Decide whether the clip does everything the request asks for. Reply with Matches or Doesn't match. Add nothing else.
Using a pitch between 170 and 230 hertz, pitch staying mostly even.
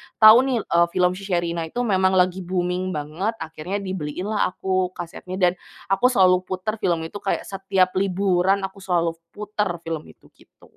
Matches